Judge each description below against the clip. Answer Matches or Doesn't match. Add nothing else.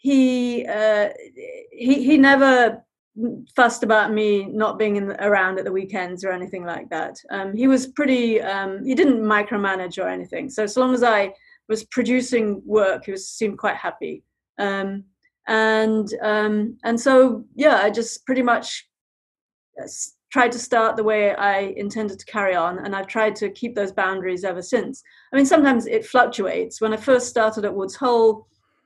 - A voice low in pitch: Doesn't match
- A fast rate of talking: Doesn't match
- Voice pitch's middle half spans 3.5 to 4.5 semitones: Matches